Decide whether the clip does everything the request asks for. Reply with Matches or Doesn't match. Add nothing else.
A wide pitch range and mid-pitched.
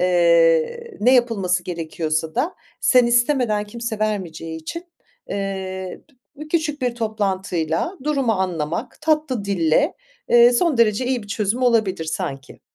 Doesn't match